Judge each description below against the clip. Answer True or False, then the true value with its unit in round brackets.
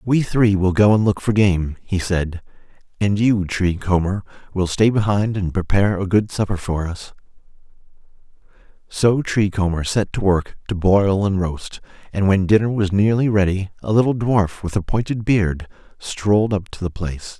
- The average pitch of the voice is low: True (100 Hz)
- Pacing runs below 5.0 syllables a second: True (4.7 syllables/s)